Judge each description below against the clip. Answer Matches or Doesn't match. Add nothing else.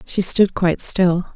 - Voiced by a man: Doesn't match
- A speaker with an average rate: Matches